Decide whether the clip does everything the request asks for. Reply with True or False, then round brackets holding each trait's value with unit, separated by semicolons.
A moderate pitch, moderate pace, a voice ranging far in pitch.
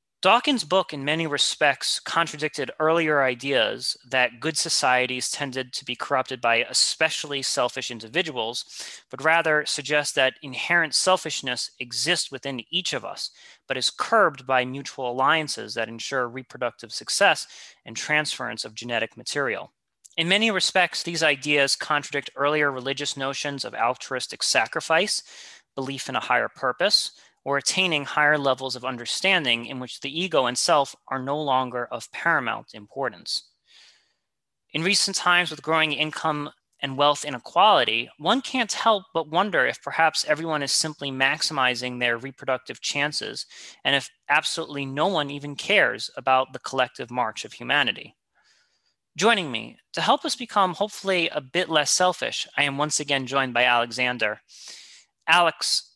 False (145 Hz; 145 wpm; 3.9 semitones)